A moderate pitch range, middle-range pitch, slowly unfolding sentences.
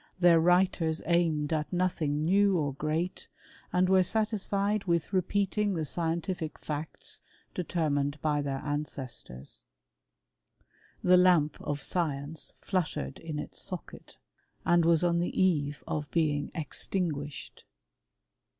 Yes: average, 3.5 semitones; medium, 165 Hz; slow, 115 wpm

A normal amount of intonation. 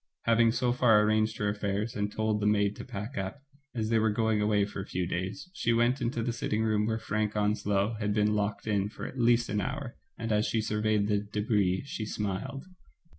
No: narrow, 1.8 semitones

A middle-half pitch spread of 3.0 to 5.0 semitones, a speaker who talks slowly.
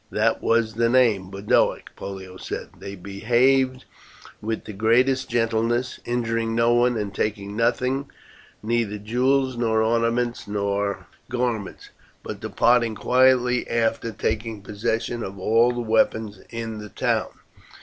No: narrow, 2.4 semitones; slow, 130 wpm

